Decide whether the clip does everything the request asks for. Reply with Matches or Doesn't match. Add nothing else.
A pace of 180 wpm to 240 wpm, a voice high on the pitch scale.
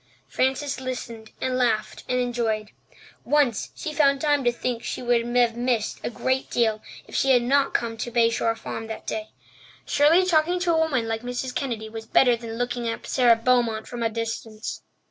Matches